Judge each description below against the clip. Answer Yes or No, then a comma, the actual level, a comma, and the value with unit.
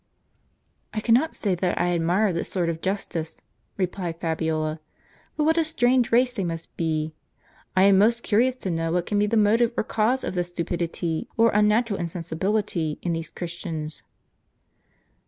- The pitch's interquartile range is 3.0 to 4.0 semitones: No, average, 4.8 semitones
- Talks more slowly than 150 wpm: No, average, 170 wpm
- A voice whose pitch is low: No, medium, 185 Hz